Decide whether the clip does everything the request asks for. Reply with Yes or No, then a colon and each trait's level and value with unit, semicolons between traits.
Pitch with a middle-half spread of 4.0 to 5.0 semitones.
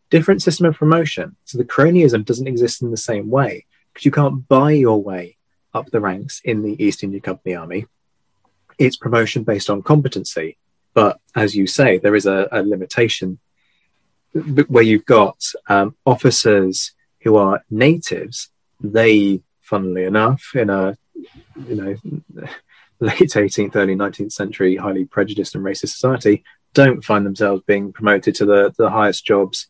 Yes: average, 4.5 semitones